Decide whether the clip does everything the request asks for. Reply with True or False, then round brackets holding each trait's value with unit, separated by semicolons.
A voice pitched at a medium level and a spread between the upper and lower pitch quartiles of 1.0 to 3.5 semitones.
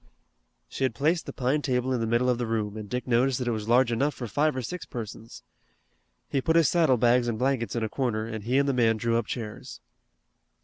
False (125 Hz; 2.8 semitones)